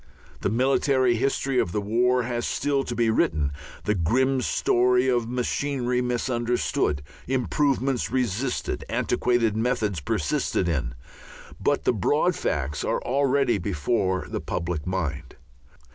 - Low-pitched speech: Yes, low, 120 Hz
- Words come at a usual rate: No, slow, 125 wpm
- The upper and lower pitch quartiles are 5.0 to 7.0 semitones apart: Yes, wide, 5.5 semitones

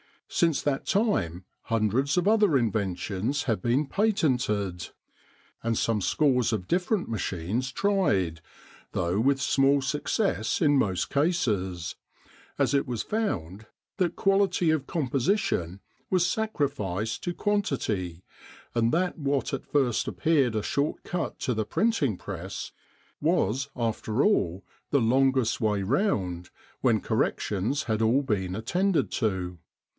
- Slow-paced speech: Yes, slow, 125 wpm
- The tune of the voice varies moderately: No, wide, 7.5 semitones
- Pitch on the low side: Yes, low, 125 Hz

